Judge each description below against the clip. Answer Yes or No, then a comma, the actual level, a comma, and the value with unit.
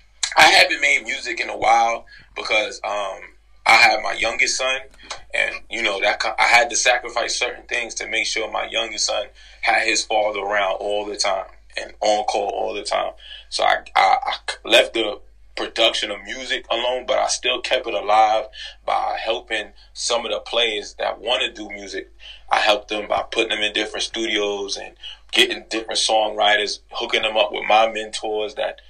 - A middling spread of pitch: No, narrow, 1.6 semitones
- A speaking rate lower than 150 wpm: No, average, 185 wpm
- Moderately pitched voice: No, low, 110 Hz